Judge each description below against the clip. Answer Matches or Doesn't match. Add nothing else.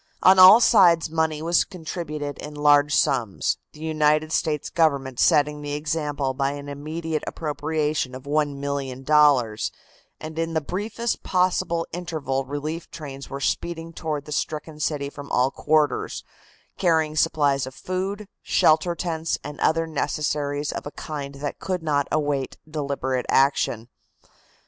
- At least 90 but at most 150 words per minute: Matches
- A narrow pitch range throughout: Matches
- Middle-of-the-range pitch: Matches